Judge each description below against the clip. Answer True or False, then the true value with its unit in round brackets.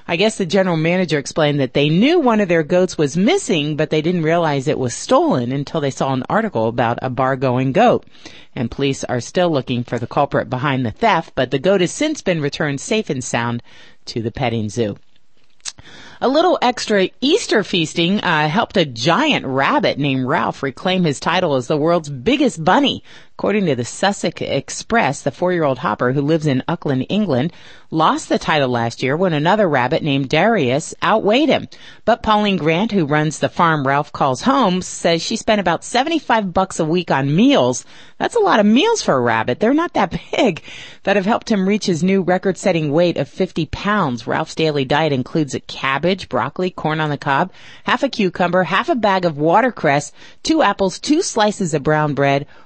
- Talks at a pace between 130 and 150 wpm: False (195 wpm)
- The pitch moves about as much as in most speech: False (6.1 semitones)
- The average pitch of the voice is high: False (165 Hz)